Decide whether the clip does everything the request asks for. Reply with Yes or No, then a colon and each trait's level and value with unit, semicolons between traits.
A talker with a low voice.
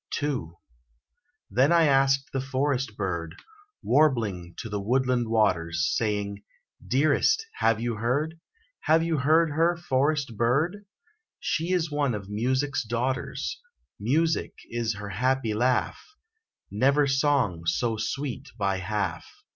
Yes: low, 130 Hz